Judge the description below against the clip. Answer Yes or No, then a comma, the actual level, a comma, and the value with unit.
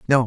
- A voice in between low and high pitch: No, low, 125 Hz